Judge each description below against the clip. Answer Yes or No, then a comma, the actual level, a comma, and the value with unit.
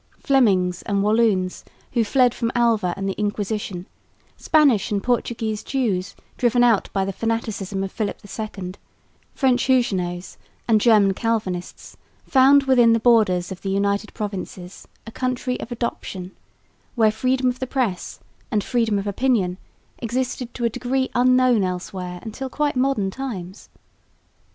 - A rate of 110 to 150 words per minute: Yes, average, 140 wpm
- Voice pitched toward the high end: Yes, high, 220 Hz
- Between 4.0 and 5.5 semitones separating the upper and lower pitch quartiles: Yes, average, 4.3 semitones